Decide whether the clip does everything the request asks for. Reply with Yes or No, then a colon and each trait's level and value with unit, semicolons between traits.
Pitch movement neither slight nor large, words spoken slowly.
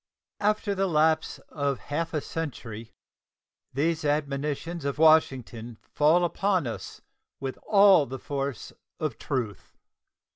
Yes: average, 3.6 semitones; slow, 115 wpm